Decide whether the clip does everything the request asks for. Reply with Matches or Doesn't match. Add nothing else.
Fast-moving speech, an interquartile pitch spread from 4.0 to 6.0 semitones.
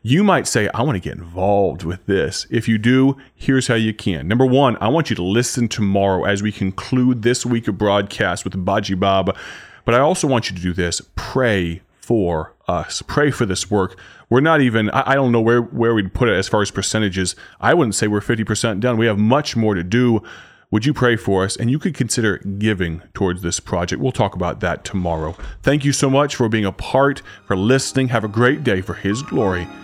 Matches